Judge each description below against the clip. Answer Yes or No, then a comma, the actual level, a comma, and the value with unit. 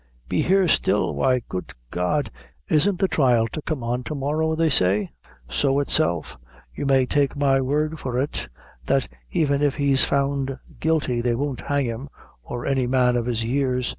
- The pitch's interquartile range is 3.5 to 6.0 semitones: No, average, 3.1 semitones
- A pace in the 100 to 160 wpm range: No, average, 175 wpm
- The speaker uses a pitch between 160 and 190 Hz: No, low, 135 Hz